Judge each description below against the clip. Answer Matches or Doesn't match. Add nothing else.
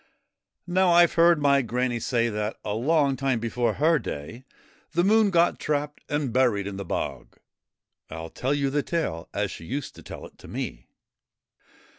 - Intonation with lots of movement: Matches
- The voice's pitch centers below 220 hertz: Matches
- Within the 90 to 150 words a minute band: Doesn't match